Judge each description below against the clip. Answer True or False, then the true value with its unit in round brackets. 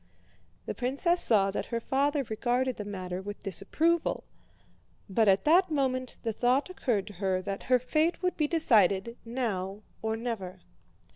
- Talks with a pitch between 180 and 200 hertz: False (235 Hz)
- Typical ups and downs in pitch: False (5.7 semitones)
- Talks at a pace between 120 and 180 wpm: True (155 wpm)